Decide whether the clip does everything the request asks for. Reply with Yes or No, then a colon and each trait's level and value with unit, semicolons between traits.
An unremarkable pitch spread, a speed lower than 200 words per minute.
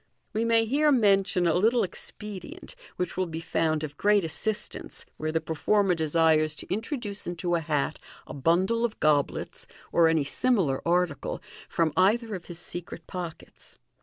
Yes: average, 4.7 semitones; average, 160 wpm